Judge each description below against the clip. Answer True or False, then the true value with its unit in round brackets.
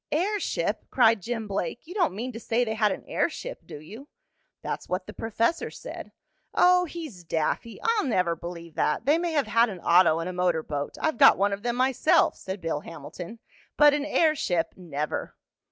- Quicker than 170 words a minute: True (190 wpm)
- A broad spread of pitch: True (8.9 semitones)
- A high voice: True (220 Hz)